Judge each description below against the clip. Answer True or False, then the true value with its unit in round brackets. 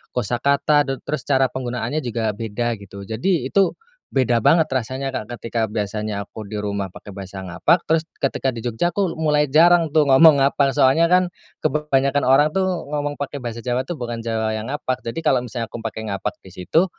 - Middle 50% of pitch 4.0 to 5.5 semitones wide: True (5.0 semitones)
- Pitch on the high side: False (130 Hz)